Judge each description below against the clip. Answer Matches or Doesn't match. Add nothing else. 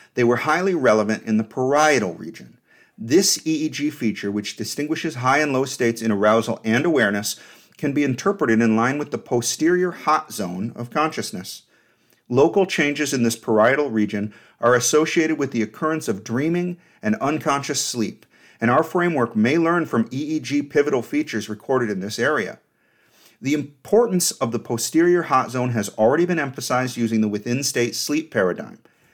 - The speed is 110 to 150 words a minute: Doesn't match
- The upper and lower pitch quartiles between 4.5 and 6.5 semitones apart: Matches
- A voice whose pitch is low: Matches